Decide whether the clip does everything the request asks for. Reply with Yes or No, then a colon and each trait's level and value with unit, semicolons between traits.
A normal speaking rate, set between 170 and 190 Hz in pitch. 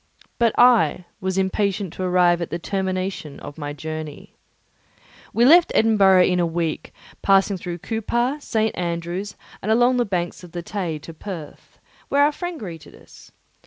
Yes: average, 165 wpm; medium, 185 Hz